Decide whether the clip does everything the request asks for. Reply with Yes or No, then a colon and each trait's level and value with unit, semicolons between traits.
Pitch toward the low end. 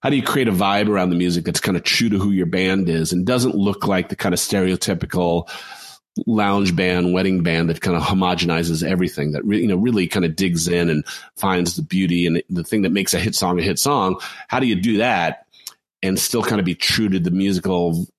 Yes: very low, 90 Hz